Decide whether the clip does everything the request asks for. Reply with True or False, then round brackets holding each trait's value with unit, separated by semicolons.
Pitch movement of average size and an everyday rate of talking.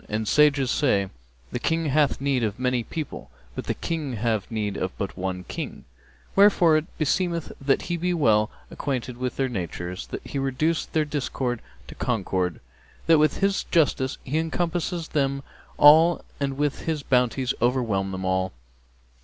False (6.0 semitones; 160 wpm)